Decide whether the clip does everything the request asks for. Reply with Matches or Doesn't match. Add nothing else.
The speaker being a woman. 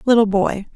Matches